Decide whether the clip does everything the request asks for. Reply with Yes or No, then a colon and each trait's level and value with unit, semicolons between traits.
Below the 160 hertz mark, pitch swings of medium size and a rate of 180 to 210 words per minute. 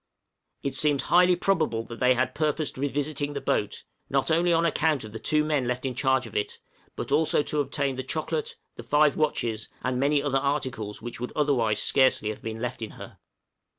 Yes: medium, 140 Hz; average, 3.6 semitones; average, 200 wpm